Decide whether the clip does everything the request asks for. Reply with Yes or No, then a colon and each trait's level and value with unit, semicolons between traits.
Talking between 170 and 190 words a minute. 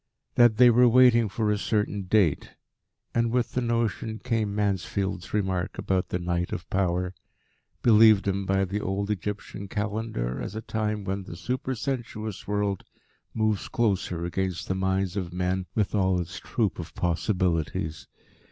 No: average, 150 wpm